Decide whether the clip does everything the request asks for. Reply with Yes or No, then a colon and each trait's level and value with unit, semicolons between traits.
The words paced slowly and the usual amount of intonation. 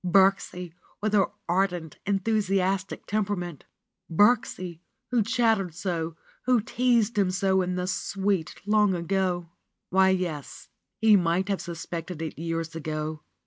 Yes: slow, 130 wpm; average, 3.2 semitones